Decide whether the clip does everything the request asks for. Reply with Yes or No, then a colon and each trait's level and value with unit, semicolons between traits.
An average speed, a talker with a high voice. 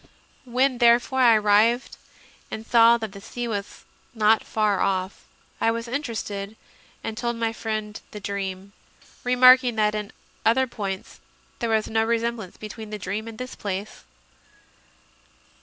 Yes: average, 150 wpm; high, 220 Hz